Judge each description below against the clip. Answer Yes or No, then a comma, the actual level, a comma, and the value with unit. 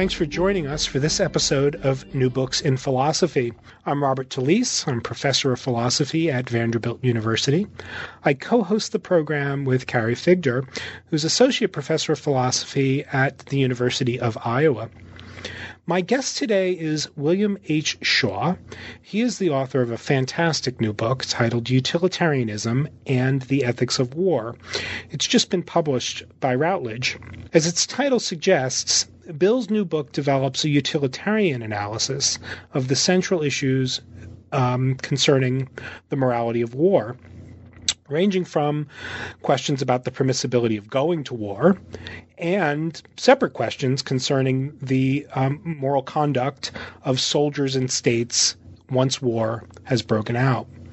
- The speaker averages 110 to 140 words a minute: Yes, slow, 135 wpm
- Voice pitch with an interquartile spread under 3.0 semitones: No, average, 4.7 semitones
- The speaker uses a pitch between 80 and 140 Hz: Yes, low, 135 Hz